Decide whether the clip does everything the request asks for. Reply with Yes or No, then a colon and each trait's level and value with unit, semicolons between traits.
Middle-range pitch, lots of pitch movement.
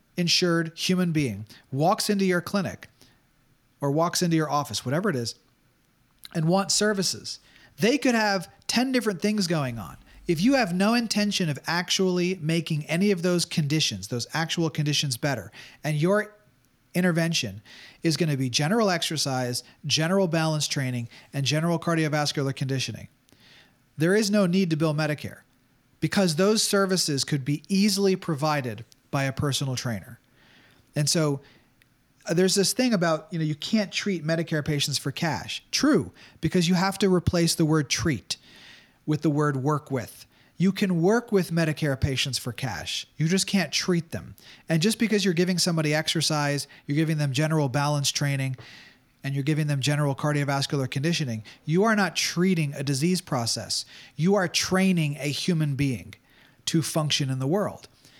No: medium, 155 Hz; average, 4.8 semitones